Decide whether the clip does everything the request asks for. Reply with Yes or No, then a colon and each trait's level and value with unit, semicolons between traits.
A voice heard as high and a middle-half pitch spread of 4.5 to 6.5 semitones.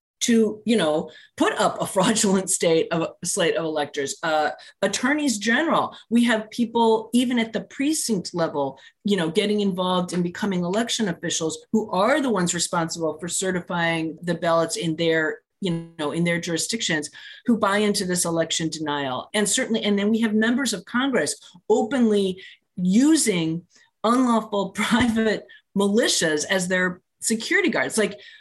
Yes: high, 195 Hz; average, 5.1 semitones